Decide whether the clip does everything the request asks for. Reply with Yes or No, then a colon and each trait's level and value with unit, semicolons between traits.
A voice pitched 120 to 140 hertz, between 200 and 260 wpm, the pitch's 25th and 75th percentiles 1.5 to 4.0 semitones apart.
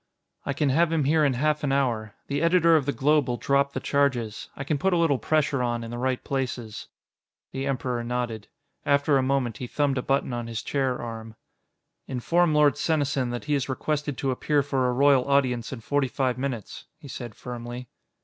Yes: low, 135 Hz; fast, 205 wpm; average, 2.7 semitones